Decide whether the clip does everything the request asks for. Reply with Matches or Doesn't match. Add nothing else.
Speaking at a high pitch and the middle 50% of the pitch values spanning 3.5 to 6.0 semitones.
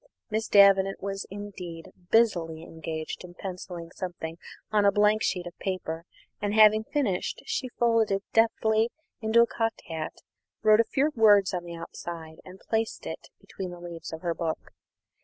Matches